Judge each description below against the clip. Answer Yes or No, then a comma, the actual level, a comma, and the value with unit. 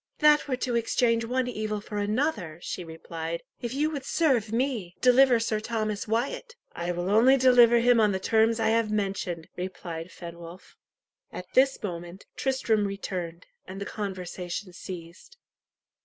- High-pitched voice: Yes, high, 215 Hz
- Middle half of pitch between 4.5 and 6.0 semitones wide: Yes, average, 5.2 semitones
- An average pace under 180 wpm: Yes, average, 155 wpm